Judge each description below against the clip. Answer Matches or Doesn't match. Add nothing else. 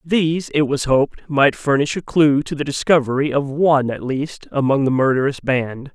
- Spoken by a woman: Doesn't match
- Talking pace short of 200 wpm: Matches